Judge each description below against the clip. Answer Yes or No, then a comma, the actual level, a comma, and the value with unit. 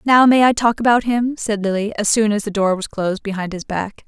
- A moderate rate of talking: No, fast, 265 wpm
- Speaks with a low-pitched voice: No, high, 215 Hz